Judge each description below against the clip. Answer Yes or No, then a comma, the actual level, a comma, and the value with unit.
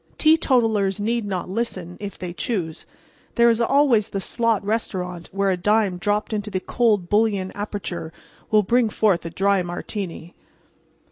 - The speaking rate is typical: Yes, average, 150 wpm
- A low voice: No, high, 205 Hz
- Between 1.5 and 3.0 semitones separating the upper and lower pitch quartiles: No, average, 3.5 semitones